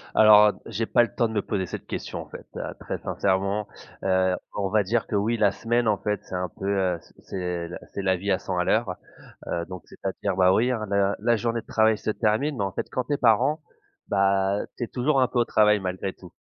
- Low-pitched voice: Yes, low, 100 Hz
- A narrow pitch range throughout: No, average, 3.2 semitones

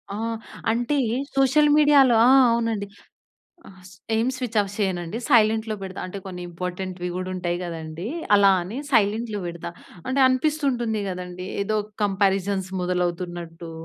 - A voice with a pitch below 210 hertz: Yes, high, 200 Hz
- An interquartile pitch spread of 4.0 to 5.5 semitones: Yes, average, 4.4 semitones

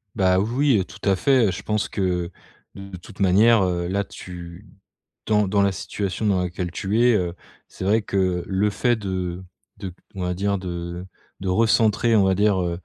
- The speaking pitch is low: Yes, very low, 95 Hz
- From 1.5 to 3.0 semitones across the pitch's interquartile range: Yes, narrow, 2.6 semitones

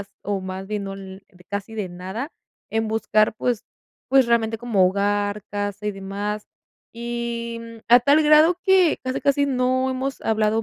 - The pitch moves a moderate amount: Yes, average, 3.8 semitones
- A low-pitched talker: No, high, 220 Hz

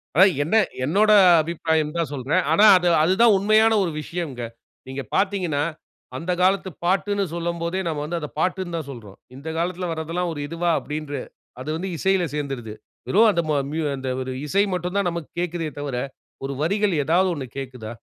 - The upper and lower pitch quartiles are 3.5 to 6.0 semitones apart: Yes, average, 3.8 semitones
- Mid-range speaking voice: Yes, medium, 170 Hz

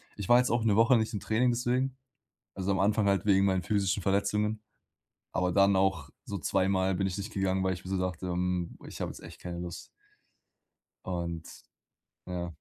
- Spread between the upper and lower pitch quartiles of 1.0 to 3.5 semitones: Yes, narrow, 2.6 semitones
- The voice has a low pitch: Yes, very low, 95 Hz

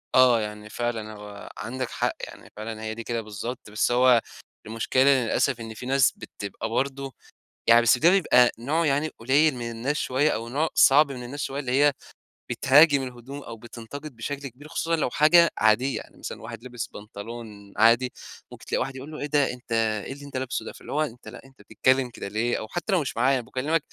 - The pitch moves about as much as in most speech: Yes, average, 3.6 semitones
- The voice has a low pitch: Yes, low, 125 Hz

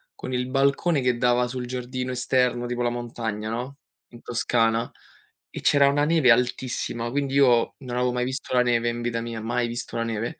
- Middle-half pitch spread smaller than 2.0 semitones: Yes, narrow, 1.4 semitones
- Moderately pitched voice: No, low, 125 Hz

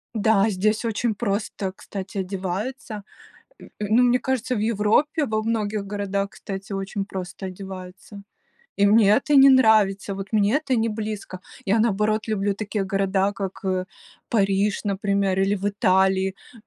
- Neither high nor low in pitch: No, high, 205 Hz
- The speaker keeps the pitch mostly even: Yes, narrow, 2.0 semitones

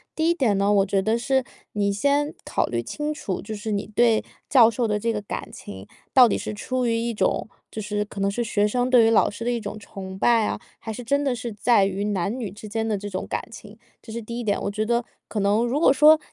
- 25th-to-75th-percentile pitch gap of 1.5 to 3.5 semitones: Yes, average, 3.0 semitones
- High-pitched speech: Yes, high, 220 Hz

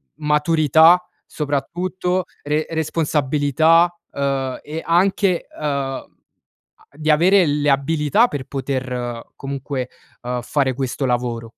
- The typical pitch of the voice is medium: Yes, medium, 145 Hz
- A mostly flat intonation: No, average, 3.4 semitones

